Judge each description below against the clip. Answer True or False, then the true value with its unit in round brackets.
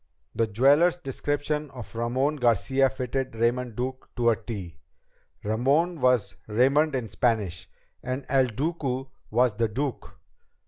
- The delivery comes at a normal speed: False (130 wpm)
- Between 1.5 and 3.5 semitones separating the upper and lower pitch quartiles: True (3.2 semitones)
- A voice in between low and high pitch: False (125 Hz)